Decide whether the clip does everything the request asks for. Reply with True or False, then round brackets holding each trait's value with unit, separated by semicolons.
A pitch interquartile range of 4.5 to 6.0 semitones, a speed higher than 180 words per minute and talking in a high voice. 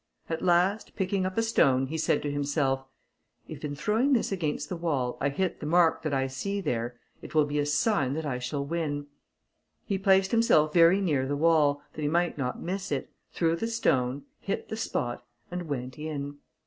False (4.8 semitones; 200 wpm; 155 Hz)